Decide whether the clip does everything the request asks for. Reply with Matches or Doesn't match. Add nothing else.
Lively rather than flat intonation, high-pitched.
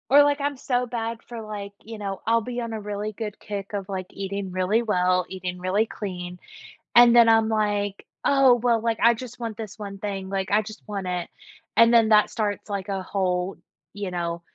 Doesn't match